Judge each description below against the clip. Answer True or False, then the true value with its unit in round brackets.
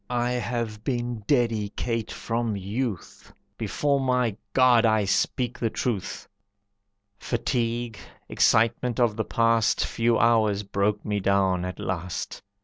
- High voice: False (115 Hz)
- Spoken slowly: True (120 wpm)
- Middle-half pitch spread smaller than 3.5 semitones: True (2.5 semitones)